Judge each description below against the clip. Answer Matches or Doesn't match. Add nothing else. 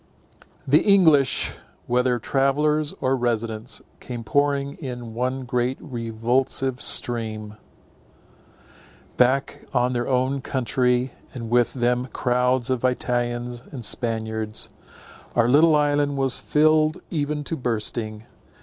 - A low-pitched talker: Matches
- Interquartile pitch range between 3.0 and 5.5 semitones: Doesn't match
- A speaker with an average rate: Doesn't match